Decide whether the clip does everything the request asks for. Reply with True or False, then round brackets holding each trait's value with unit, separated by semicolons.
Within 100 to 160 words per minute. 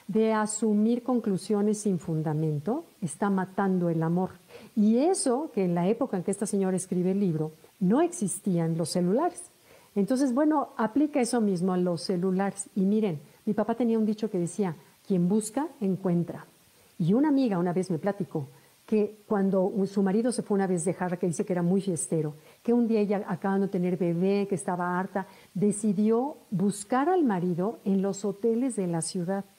False (180 wpm)